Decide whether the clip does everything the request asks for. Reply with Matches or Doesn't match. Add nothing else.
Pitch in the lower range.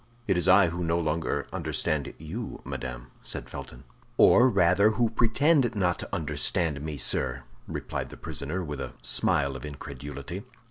Matches